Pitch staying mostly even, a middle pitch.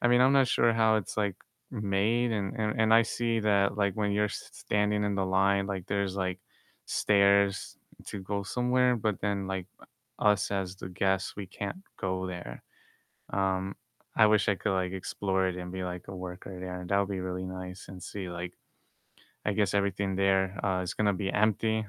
No: narrow, 2.0 semitones; low, 100 Hz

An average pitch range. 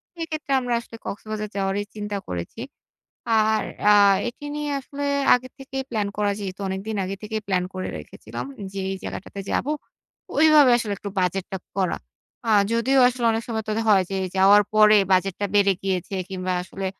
Yes: average, 3.5 semitones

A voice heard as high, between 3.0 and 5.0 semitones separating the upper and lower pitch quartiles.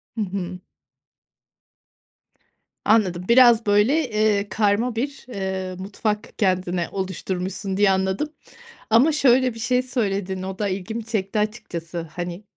Yes: high, 205 Hz; average, 3.3 semitones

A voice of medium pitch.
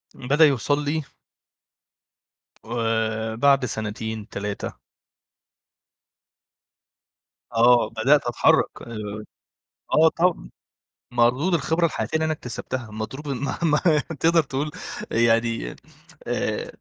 No: low, 120 Hz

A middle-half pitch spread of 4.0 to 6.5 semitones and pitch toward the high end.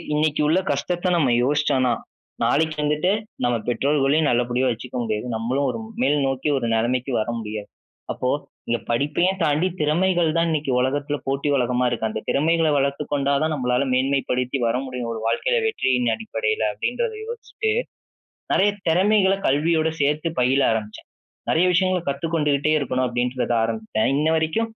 No: average, 4.4 semitones; medium, 140 Hz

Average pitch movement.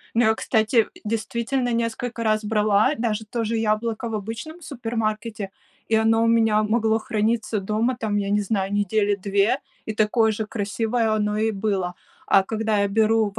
No: narrow, 1.6 semitones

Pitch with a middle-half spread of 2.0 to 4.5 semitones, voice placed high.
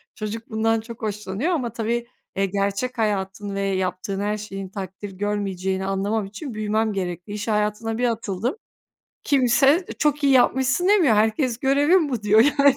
Yes: average, 3.9 semitones; high, 215 Hz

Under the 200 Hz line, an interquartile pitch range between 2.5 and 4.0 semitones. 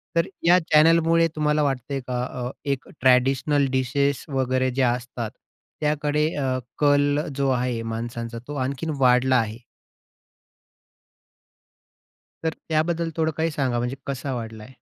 Yes: low, 135 Hz; average, 3.2 semitones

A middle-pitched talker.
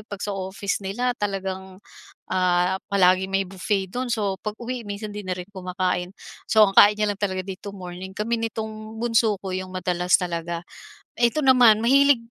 No: high, 195 Hz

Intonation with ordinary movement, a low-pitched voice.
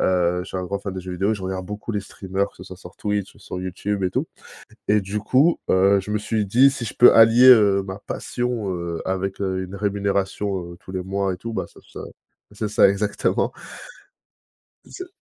No: narrow, 2.0 semitones; low, 100 Hz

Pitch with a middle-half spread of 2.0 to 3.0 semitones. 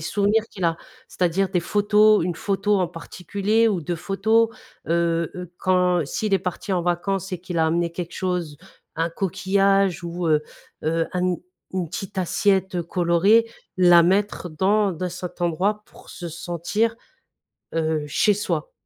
Yes: average, 2.7 semitones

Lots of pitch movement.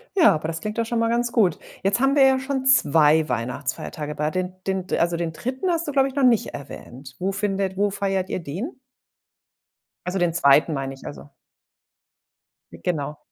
Yes: wide, 7.7 semitones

